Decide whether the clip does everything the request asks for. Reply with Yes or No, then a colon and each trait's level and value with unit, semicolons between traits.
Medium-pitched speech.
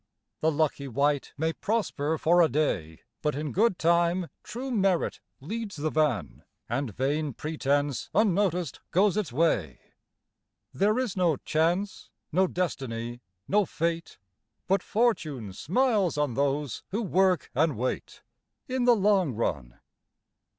Yes: medium, 160 Hz